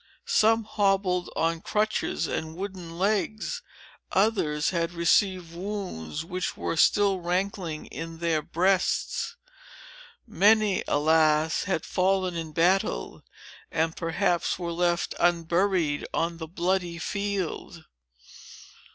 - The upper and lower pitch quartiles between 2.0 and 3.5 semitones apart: Yes, average, 2.9 semitones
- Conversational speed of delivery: No, slow, 105 wpm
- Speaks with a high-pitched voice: No, medium, 175 Hz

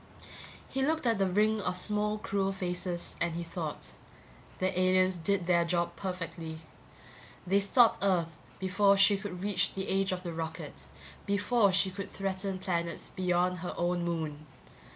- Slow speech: No, average, 155 wpm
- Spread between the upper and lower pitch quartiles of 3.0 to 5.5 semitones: No, narrow, 2.5 semitones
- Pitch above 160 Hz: Yes, medium, 185 Hz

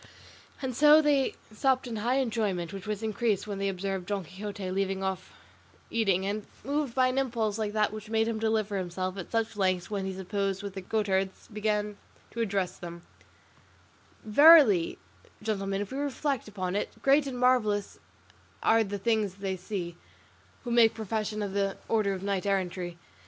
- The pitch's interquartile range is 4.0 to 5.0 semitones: No, average, 2.8 semitones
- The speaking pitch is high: Yes, high, 210 Hz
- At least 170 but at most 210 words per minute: Yes, average, 175 wpm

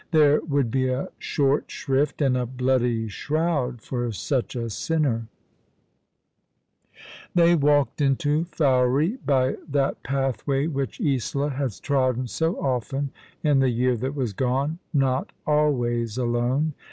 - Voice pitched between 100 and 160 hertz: Yes, low, 135 Hz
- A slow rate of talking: Yes, slow, 130 wpm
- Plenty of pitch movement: No, average, 2.8 semitones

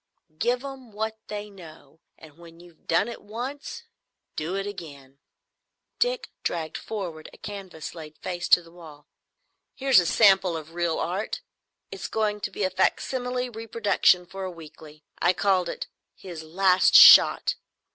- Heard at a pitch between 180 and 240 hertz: Yes, medium, 185 Hz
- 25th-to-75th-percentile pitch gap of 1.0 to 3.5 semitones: No, average, 4.6 semitones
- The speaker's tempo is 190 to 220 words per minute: No, average, 155 wpm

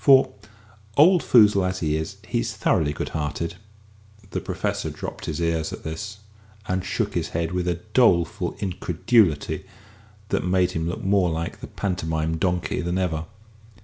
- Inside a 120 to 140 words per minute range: No, average, 155 wpm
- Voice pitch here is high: No, very low, 90 Hz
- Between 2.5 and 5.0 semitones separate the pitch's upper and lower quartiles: Yes, average, 2.8 semitones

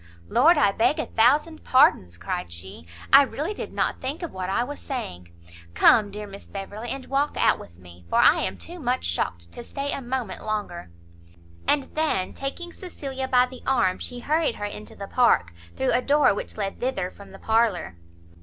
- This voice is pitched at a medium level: No, high, 235 Hz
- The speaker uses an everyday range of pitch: No, wide, 6.5 semitones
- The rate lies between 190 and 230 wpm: Yes, average, 195 wpm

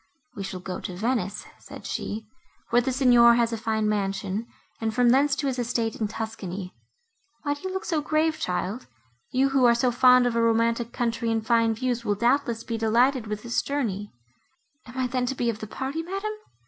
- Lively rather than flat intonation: No, average, 2.9 semitones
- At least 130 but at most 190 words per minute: No, average, 200 wpm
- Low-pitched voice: No, high, 235 Hz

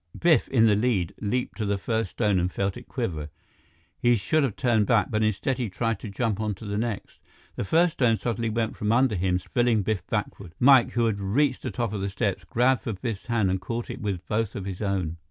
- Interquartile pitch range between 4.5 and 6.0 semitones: No, average, 3.6 semitones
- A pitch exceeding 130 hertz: No, low, 110 Hz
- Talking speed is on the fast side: Yes, fast, 235 wpm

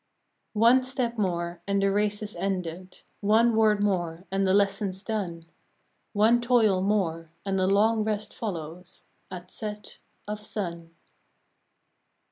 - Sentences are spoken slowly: Yes, slow, 130 wpm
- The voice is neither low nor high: No, high, 200 Hz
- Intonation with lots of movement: No, average, 2.8 semitones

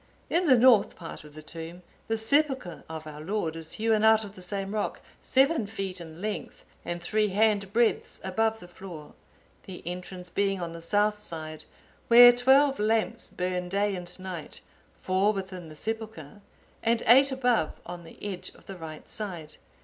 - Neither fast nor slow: Yes, average, 175 wpm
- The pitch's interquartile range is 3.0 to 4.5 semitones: Yes, average, 4.2 semitones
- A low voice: No, high, 195 Hz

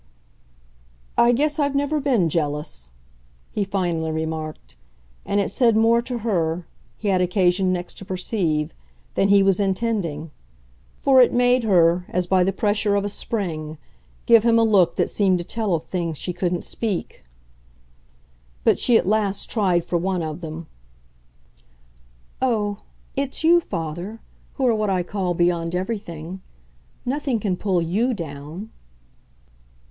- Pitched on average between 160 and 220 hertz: Yes, high, 190 Hz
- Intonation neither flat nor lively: Yes, average, 4.7 semitones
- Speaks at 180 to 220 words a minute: No, average, 150 wpm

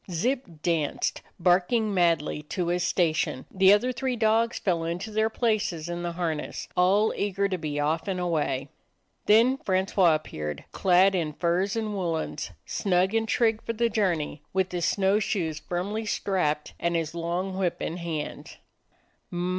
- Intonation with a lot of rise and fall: No, average, 3.8 semitones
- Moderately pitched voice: Yes, medium, 180 Hz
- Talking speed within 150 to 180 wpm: Yes, average, 155 wpm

